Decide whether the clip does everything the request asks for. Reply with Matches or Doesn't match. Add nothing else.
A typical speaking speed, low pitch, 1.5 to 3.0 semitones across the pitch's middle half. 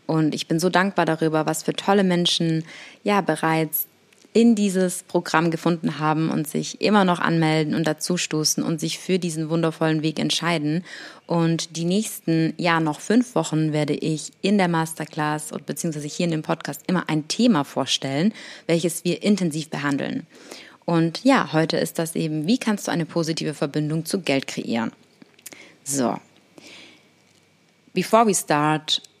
Doesn't match